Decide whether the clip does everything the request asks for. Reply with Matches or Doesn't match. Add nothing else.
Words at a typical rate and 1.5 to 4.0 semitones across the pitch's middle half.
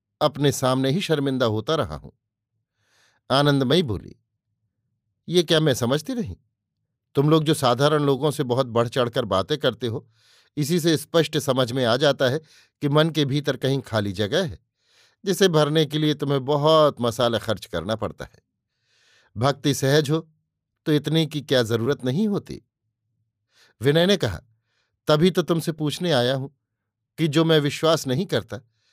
Doesn't match